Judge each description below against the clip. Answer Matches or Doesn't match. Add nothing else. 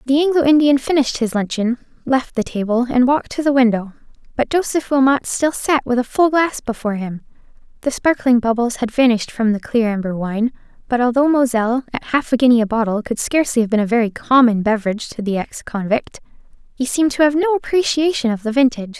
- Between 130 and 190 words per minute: Doesn't match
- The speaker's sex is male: Doesn't match